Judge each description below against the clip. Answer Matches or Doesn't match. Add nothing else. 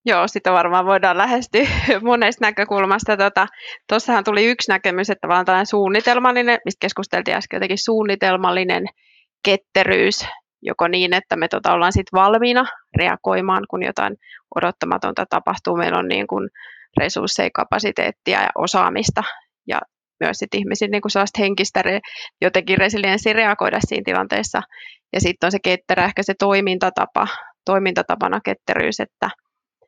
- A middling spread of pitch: Doesn't match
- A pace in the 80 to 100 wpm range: Doesn't match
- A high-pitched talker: Matches